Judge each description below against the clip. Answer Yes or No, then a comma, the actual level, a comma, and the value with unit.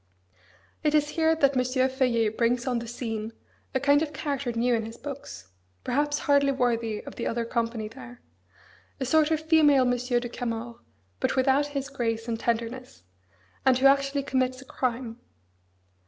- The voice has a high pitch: Yes, very high, 255 Hz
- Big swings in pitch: No, average, 3.1 semitones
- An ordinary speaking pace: Yes, average, 170 wpm